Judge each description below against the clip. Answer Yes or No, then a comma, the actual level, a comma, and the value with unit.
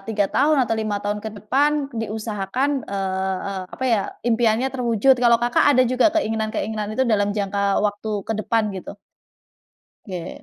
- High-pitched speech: Yes, high, 220 Hz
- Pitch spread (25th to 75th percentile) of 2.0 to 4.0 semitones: Yes, average, 2.9 semitones